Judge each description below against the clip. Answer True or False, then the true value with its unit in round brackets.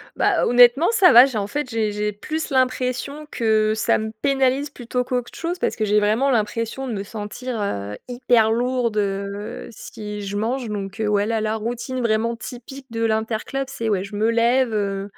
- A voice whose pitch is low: False (230 Hz)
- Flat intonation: False (3.2 semitones)